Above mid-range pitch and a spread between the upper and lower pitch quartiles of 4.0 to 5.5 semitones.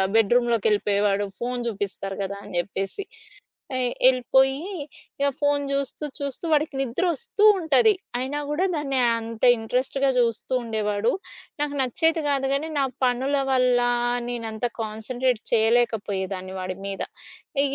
Yes: high, 245 Hz; average, 4.4 semitones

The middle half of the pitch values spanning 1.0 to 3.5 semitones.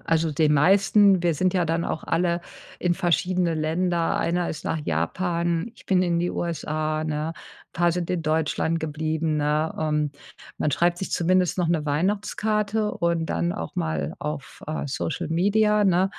Yes: narrow, 2.6 semitones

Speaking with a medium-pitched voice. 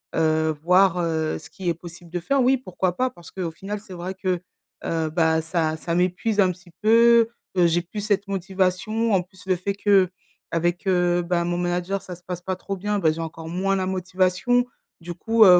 Yes: medium, 180 Hz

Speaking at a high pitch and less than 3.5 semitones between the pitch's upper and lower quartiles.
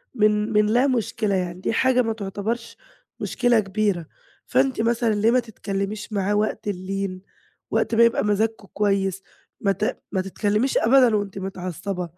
Yes: high, 210 Hz; average, 2.8 semitones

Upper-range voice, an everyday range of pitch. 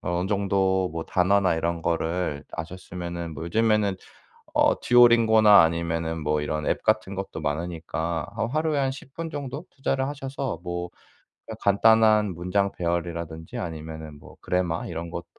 No: very low, 90 Hz; average, 4.8 semitones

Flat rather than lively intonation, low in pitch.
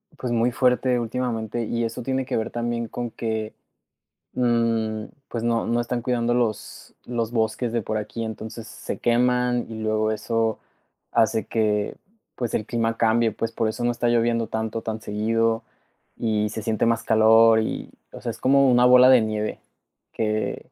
Yes: narrow, 1.4 semitones; low, 115 Hz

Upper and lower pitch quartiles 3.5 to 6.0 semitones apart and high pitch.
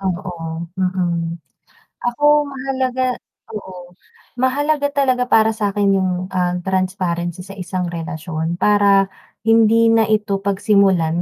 Yes: average, 3.8 semitones; high, 195 Hz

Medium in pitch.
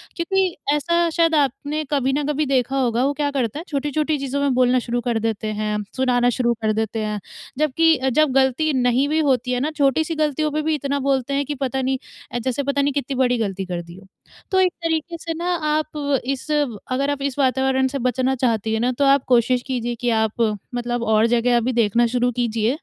No: very high, 265 Hz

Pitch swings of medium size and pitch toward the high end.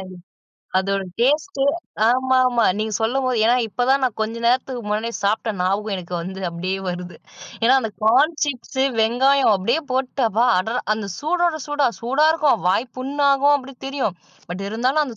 Yes: average, 4.2 semitones; high, 245 Hz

